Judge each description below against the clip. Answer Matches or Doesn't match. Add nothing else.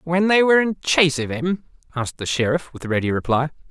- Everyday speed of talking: Doesn't match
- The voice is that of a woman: Doesn't match